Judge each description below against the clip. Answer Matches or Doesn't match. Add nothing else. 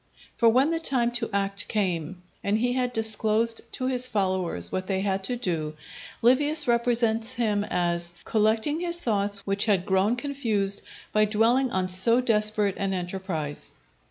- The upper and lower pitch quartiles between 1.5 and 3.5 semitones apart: Doesn't match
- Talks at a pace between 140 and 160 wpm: Matches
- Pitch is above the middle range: Matches